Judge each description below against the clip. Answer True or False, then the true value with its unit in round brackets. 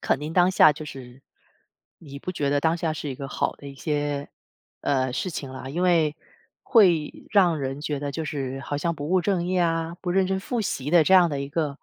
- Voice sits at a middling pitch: True (155 Hz)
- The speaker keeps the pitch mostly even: False (3.8 semitones)